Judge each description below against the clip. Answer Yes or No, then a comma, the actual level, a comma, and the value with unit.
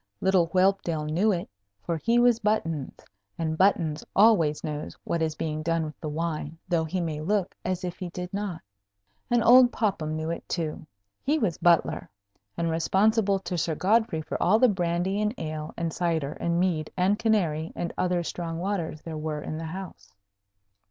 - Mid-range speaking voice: Yes, medium, 170 Hz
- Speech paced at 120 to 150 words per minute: No, average, 180 wpm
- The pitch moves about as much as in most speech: Yes, average, 3.7 semitones